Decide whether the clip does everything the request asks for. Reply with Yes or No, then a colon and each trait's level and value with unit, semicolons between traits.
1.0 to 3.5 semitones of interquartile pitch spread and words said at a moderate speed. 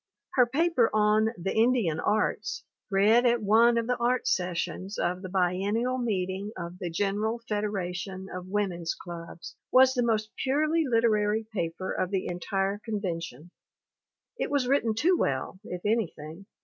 No: average, 4.3 semitones; average, 150 wpm